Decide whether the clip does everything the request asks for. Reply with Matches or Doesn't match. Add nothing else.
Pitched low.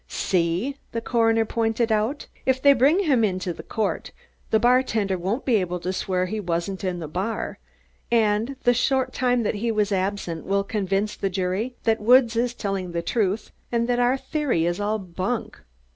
Doesn't match